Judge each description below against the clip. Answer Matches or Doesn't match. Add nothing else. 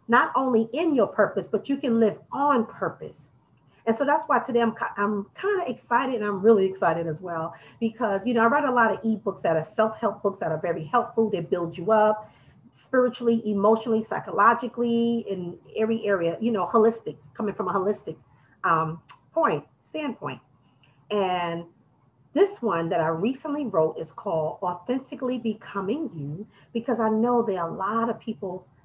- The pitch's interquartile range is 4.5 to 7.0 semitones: Matches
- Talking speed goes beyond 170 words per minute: Matches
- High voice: Matches